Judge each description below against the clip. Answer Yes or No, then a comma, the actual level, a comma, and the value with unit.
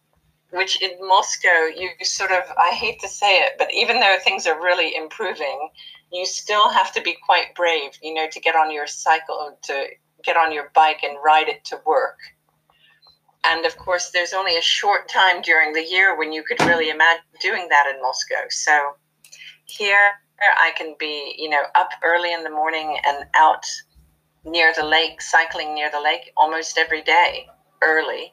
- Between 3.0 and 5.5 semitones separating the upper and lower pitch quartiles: Yes, average, 3.3 semitones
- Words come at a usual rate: Yes, average, 185 wpm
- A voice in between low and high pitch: Yes, medium, 160 Hz